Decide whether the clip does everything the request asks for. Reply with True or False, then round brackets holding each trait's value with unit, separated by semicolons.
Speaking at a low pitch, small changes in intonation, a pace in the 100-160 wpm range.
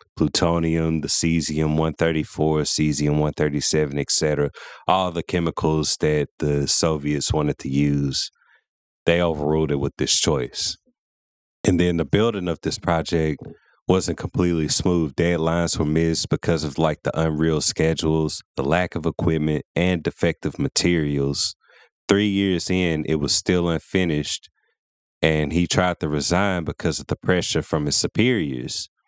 True (80 Hz; 2.1 semitones; 140 wpm)